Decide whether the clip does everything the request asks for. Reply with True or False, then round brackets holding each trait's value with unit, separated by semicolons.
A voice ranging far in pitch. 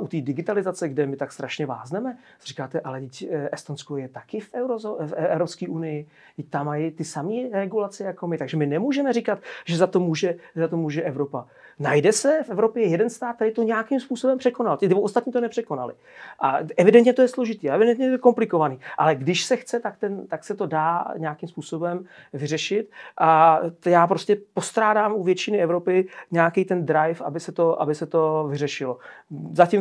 True (5.7 semitones)